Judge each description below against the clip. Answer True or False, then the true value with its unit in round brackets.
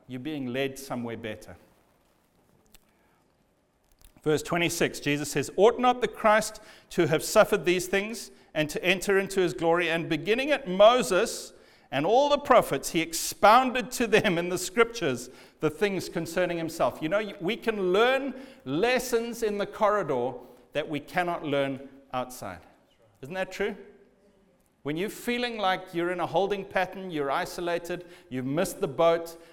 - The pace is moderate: True (150 wpm)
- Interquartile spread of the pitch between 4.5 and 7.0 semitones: True (5.5 semitones)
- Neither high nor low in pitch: True (180 Hz)